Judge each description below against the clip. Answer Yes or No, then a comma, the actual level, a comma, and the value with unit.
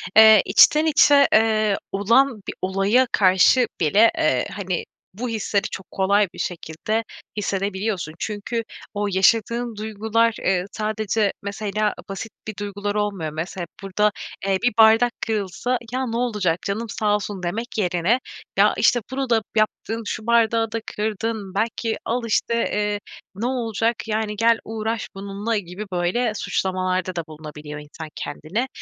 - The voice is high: Yes, high, 210 Hz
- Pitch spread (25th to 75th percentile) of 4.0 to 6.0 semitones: No, average, 3.0 semitones